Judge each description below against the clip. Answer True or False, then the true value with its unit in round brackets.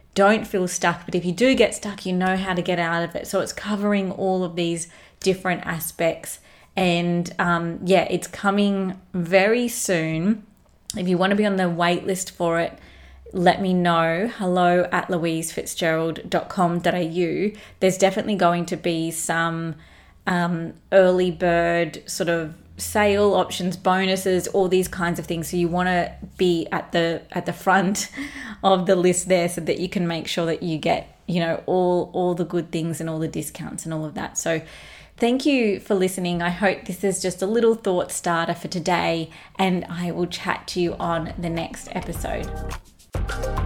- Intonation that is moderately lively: False (2.0 semitones)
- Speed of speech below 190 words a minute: True (180 wpm)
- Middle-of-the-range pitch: True (180 Hz)